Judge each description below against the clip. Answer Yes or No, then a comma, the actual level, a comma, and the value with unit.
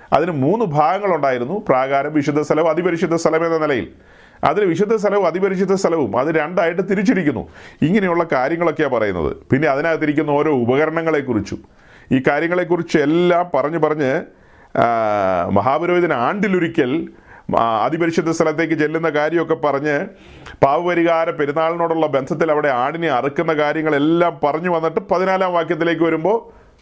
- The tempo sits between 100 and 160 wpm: Yes, average, 110 wpm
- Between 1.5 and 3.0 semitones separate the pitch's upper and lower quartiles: Yes, narrow, 2.4 semitones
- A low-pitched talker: No, medium, 165 Hz